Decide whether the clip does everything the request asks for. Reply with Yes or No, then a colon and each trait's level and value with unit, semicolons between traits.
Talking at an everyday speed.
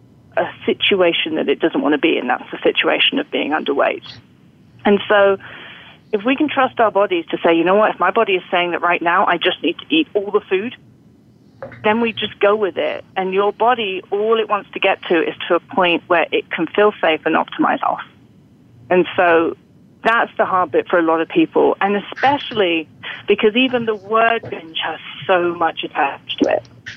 No: fast, 210 wpm